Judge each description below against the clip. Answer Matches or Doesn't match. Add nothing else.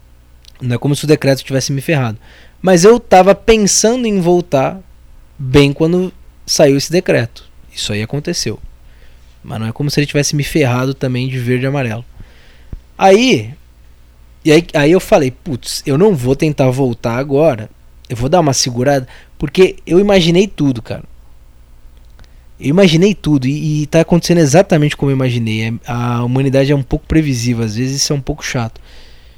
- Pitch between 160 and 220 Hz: Doesn't match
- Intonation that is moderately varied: Doesn't match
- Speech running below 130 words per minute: Doesn't match